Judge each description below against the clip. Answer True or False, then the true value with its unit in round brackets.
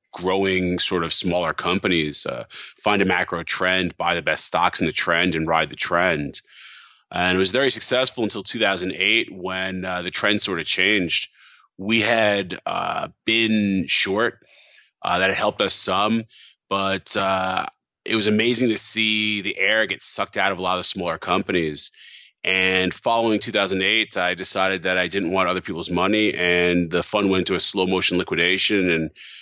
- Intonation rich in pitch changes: False (2.9 semitones)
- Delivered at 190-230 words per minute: False (175 wpm)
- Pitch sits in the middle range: False (95 Hz)